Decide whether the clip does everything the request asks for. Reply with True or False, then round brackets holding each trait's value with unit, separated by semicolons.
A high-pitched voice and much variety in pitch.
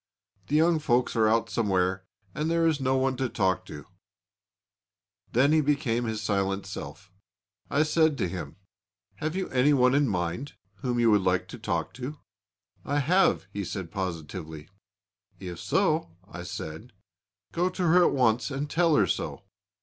False (120 Hz; 7.8 semitones)